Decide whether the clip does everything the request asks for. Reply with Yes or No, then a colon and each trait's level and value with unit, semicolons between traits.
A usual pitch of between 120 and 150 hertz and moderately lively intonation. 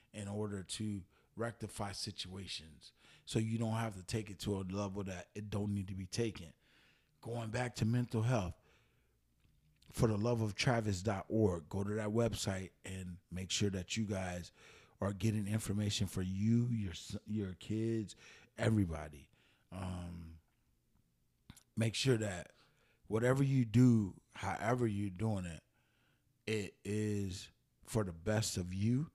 No: low, 105 Hz; average, 3.3 semitones